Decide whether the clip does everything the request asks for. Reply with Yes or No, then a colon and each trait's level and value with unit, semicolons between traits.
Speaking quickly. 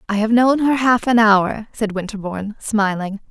No: average, 180 wpm